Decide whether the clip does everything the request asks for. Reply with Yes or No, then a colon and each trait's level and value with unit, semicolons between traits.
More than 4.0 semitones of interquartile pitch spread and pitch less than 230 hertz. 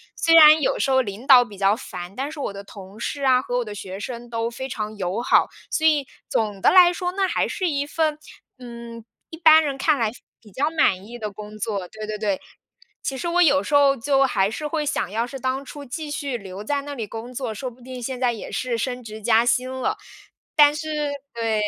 No: average, 5.0 semitones; very high, 250 Hz